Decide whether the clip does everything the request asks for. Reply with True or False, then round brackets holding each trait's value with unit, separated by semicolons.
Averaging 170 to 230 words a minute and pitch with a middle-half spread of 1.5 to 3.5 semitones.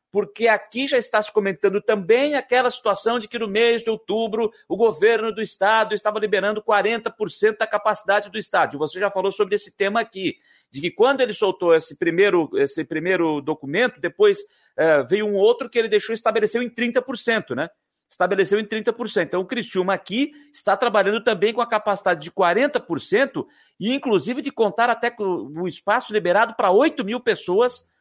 True (180 wpm; 3.2 semitones)